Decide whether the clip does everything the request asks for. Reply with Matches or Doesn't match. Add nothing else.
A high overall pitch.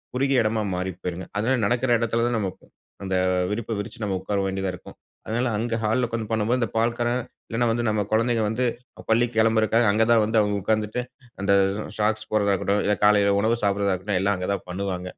Doesn't match